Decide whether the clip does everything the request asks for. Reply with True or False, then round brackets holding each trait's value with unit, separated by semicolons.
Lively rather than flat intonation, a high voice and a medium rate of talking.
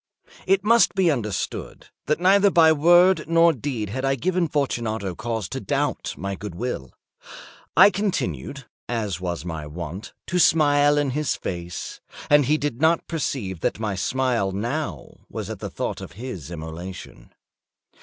False (8.8 semitones; 130 Hz; 155 wpm)